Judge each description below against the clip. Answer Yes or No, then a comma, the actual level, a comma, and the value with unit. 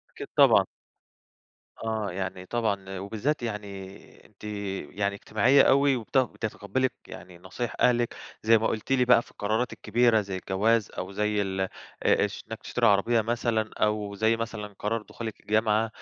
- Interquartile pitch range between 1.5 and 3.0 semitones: Yes, narrow, 2.5 semitones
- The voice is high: No, low, 110 Hz